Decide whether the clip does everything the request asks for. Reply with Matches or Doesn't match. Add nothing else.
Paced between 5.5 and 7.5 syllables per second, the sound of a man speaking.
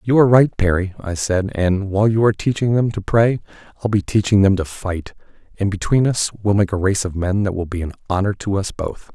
Matches